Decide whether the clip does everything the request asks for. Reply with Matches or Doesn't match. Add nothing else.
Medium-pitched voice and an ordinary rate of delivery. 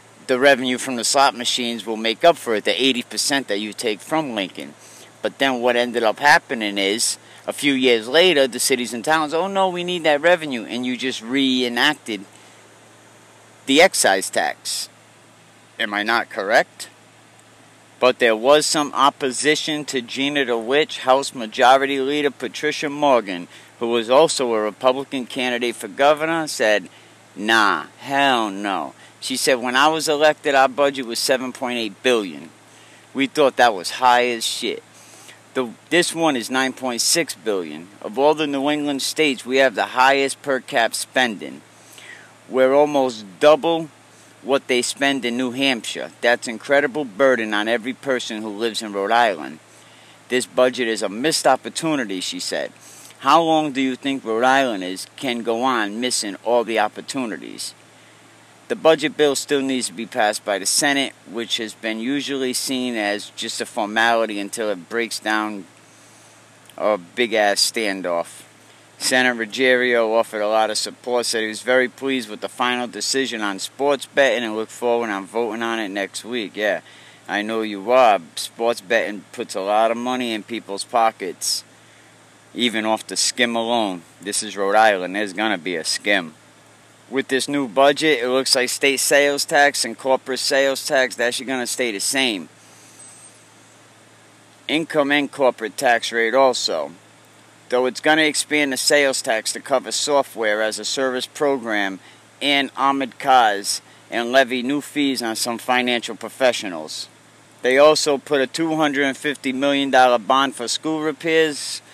Doesn't match